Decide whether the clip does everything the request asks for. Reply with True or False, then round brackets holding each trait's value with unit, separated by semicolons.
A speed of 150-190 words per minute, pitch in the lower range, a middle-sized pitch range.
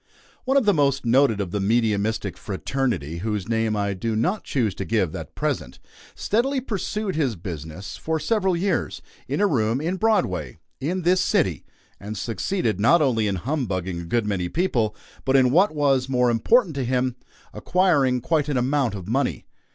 False (175 wpm; 125 Hz; 7.6 semitones)